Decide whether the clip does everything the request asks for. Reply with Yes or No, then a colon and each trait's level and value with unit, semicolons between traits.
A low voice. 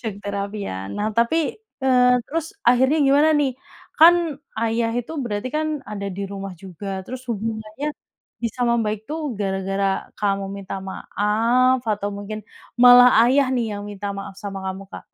No: high, 220 Hz